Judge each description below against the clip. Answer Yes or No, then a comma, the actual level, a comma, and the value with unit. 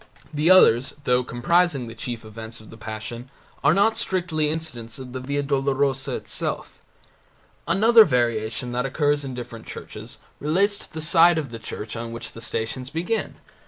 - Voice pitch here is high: No, low, 135 Hz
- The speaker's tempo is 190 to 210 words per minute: No, average, 165 wpm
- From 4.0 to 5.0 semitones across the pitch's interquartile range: No, wide, 5.5 semitones